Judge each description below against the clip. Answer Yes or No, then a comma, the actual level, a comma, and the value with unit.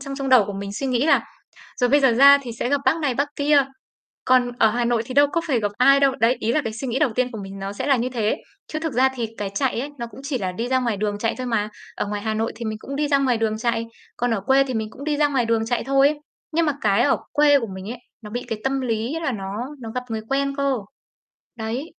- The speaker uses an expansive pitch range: No, average, 3.7 semitones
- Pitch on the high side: Yes, high, 245 Hz